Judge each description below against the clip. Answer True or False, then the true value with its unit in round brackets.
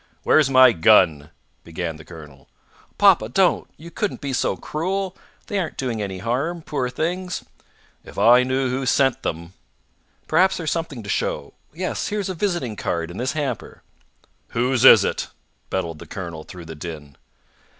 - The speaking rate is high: False (165 wpm)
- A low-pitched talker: True (125 Hz)